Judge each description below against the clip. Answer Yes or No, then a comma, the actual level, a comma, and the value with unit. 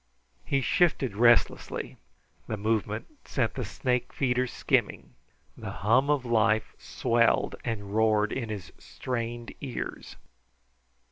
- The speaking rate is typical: No, slow, 115 wpm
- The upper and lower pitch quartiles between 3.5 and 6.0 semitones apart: No, average, 2.7 semitones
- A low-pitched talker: Yes, low, 115 Hz